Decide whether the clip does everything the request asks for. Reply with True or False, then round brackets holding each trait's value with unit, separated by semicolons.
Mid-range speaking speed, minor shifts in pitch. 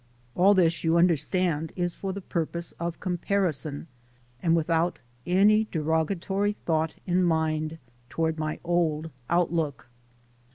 False (125 wpm; 2.2 semitones)